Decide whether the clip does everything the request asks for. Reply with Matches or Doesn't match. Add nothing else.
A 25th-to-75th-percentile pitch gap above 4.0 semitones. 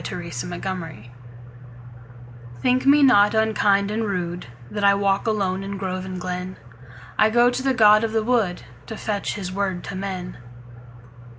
Doesn't match